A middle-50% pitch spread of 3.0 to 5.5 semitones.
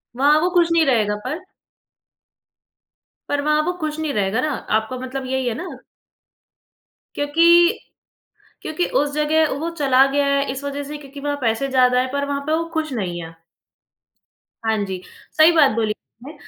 Yes: average, 3.5 semitones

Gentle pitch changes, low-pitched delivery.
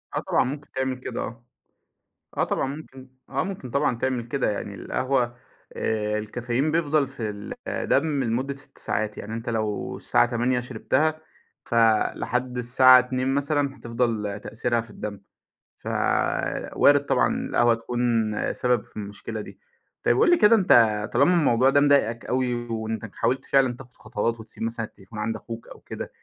No: average, 3.0 semitones; low, 120 Hz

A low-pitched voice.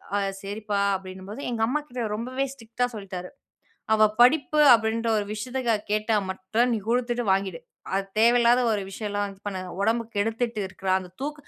No: high, 220 Hz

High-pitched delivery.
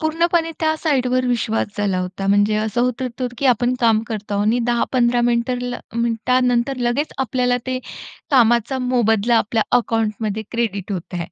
Yes: high, 240 Hz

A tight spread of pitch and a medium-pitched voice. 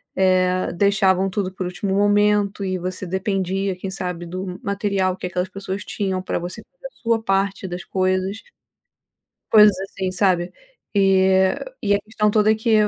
No: narrow, 1.6 semitones; high, 195 Hz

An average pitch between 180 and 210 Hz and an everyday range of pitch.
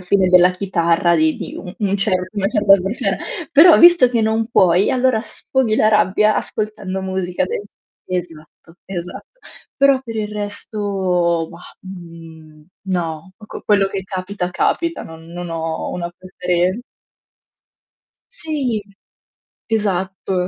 Yes: high, 190 Hz; average, 3.4 semitones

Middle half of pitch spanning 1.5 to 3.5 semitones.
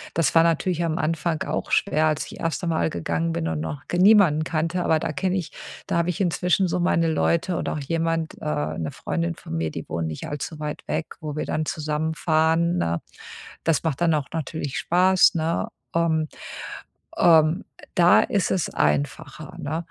Yes: narrow, 2.4 semitones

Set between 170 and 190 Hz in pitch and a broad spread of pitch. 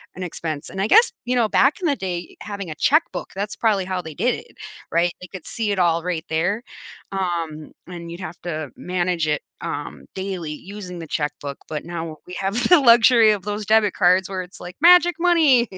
No: medium, 185 Hz; average, 4.3 semitones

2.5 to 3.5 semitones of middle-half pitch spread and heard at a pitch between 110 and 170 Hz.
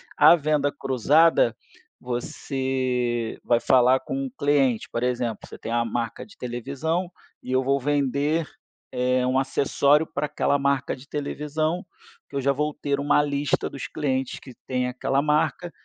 Yes: average, 2.8 semitones; medium, 140 Hz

